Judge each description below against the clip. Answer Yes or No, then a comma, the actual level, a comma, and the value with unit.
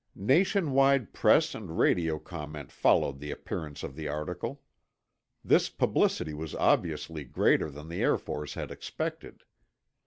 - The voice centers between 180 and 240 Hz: No, very low, 80 Hz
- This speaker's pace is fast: No, slow, 135 wpm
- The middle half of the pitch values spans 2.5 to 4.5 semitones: No, wide, 5.5 semitones